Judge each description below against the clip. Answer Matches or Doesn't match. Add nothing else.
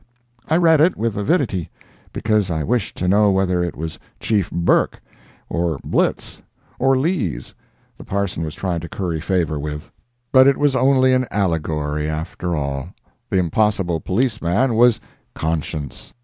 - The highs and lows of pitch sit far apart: Matches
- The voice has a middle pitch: Doesn't match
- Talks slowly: Doesn't match